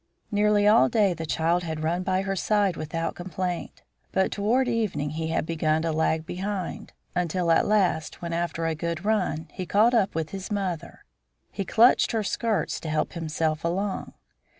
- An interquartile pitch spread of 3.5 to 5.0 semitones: Yes, average, 4.0 semitones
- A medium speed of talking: Yes, average, 175 wpm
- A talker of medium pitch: Yes, medium, 175 Hz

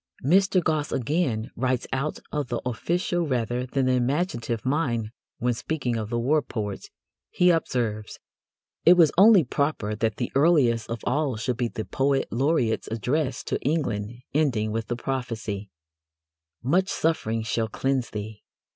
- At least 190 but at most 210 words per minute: No, average, 150 wpm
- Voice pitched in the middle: No, low, 125 Hz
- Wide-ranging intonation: No, average, 5.0 semitones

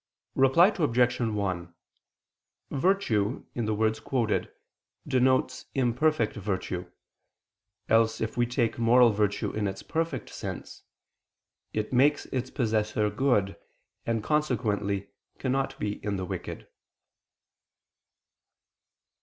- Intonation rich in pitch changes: No, average, 3.8 semitones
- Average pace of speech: No, slow, 105 wpm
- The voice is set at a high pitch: No, low, 115 Hz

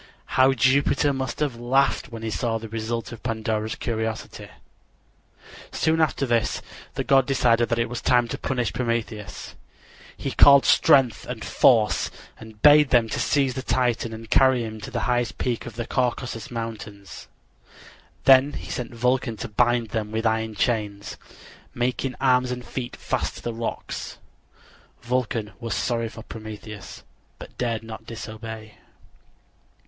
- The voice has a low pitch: Yes, low, 115 Hz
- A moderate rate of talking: Yes, average, 150 wpm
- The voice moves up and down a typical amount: No, narrow, 2.3 semitones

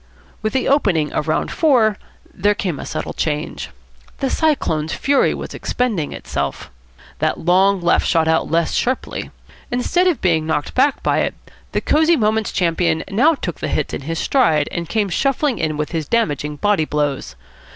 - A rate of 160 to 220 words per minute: Yes, average, 170 wpm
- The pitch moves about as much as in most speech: No, wide, 7.9 semitones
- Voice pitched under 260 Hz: Yes, medium, 185 Hz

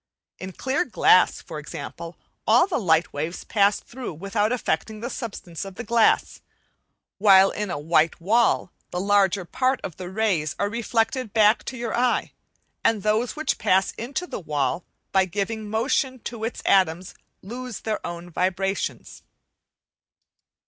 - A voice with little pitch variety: No, average, 4.5 semitones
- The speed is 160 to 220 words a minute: No, average, 150 wpm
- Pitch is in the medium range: No, high, 205 Hz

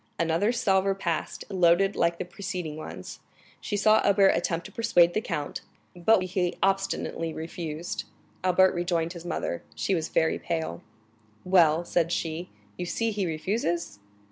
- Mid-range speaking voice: Yes, medium, 175 Hz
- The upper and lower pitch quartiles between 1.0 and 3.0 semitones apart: Yes, average, 2.7 semitones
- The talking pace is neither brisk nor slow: Yes, average, 145 wpm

